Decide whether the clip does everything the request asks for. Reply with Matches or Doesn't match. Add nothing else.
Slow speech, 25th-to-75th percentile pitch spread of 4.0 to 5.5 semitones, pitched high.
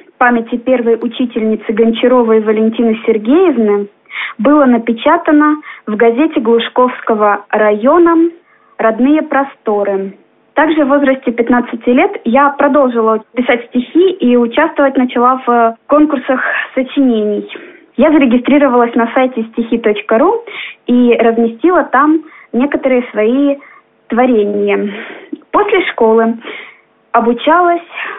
Matches